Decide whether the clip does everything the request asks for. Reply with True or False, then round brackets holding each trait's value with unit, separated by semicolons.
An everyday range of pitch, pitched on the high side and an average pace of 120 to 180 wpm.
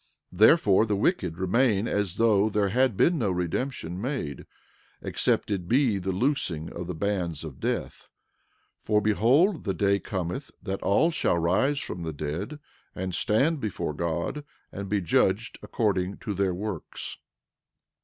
False (4.7 semitones; 100 Hz; 155 wpm)